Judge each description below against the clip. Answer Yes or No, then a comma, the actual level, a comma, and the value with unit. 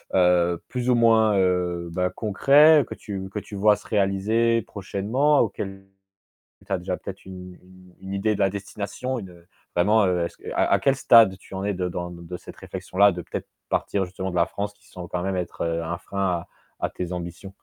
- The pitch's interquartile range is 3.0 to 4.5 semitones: No, narrow, 2.6 semitones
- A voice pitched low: Yes, very low, 95 Hz